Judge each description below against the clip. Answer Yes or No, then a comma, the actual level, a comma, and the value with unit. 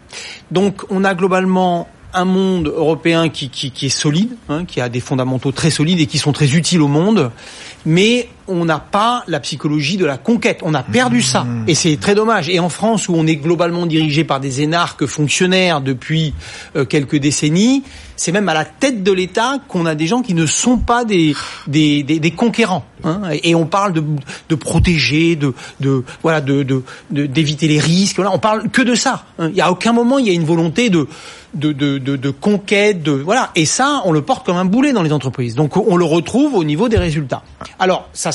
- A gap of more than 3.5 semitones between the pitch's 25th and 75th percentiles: Yes, average, 4.6 semitones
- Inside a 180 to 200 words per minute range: No, average, 215 wpm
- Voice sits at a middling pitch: Yes, medium, 165 Hz